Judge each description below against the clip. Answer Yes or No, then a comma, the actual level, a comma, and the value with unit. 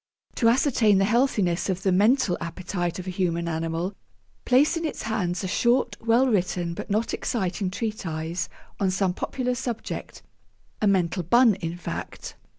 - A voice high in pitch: Yes, high, 195 Hz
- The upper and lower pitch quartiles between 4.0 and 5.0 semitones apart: Yes, average, 4.7 semitones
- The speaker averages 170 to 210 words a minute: No, average, 155 wpm